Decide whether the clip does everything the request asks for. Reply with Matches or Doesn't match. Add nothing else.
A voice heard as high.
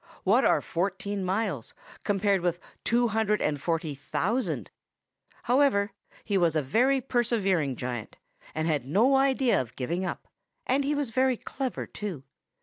Matches